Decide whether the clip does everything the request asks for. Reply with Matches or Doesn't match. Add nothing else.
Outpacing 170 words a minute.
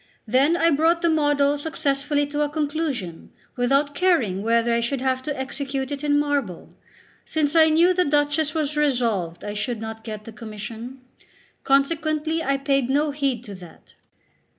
Doesn't match